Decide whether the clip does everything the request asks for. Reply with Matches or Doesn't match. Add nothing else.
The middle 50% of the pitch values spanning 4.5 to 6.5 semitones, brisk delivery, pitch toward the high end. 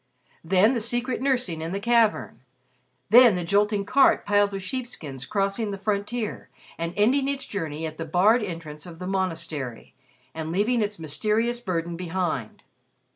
Doesn't match